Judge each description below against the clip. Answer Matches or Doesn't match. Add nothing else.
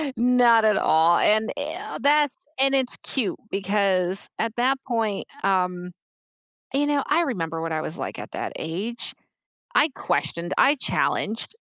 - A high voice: Matches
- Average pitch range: Doesn't match